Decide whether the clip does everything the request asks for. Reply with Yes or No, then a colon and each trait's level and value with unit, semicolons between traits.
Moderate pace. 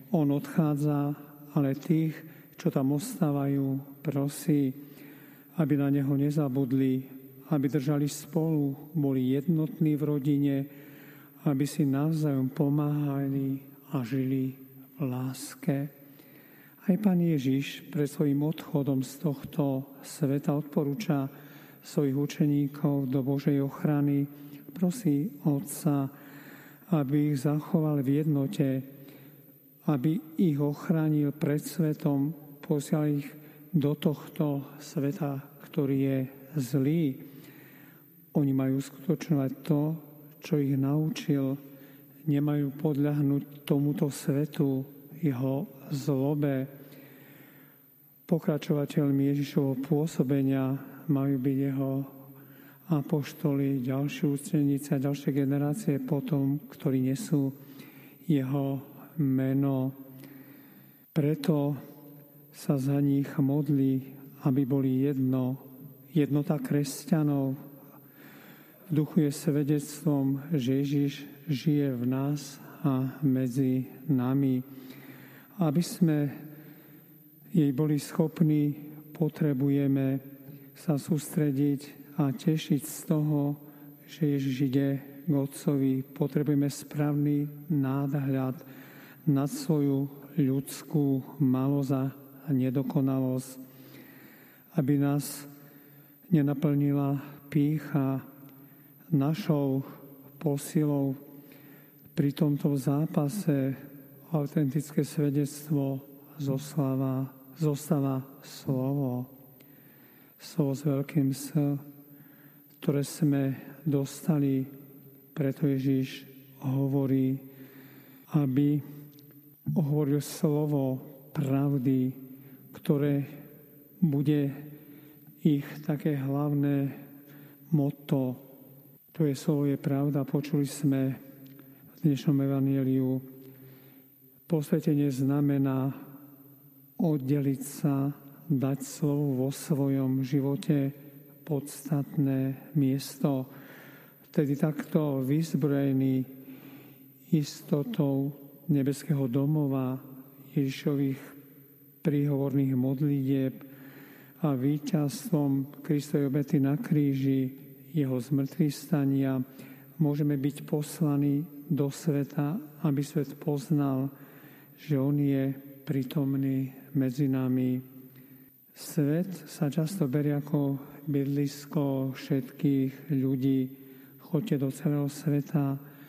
No: slow, 80 wpm